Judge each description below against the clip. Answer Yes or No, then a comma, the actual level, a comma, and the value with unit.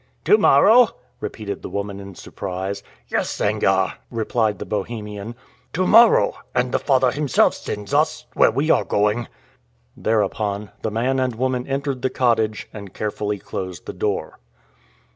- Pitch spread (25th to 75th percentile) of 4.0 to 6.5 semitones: Yes, average, 4.3 semitones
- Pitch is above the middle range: No, low, 110 Hz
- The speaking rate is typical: Yes, average, 145 wpm